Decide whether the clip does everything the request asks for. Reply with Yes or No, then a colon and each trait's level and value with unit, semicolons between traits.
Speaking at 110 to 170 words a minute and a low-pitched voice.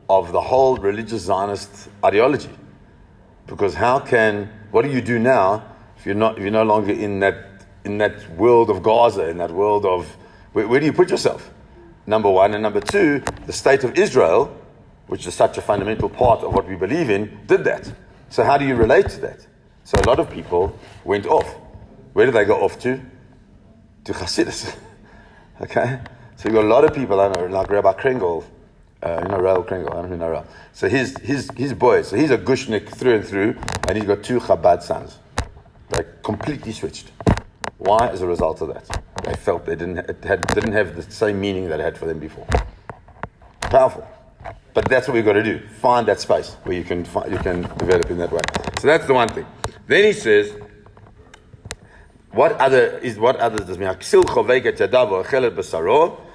No: average, 195 wpm; low, 110 Hz